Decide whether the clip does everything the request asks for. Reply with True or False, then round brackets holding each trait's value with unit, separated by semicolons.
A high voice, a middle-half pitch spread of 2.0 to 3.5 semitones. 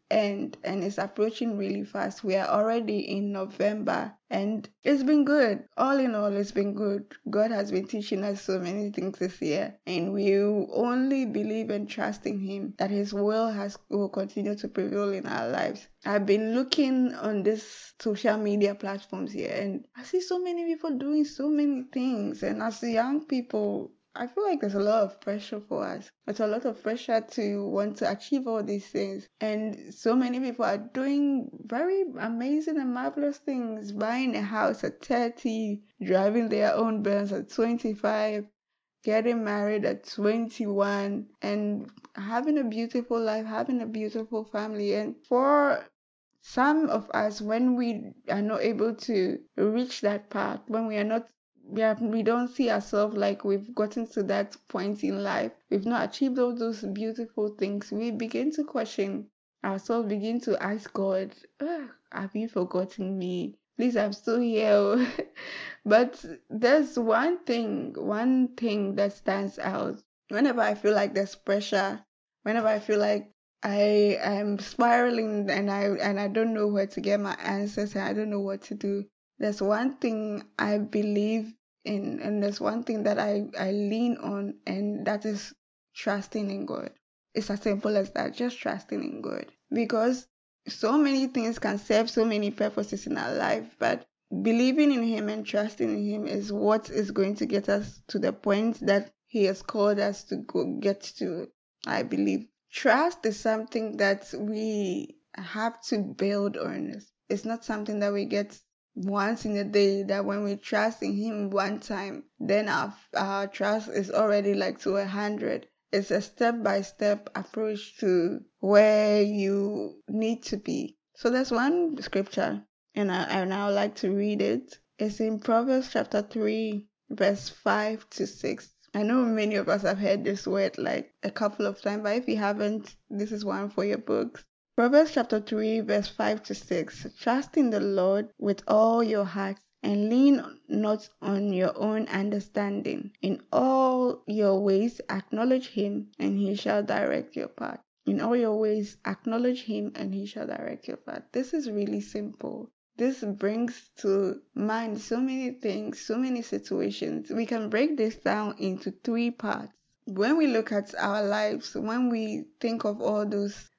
True (215 Hz; 2.6 semitones)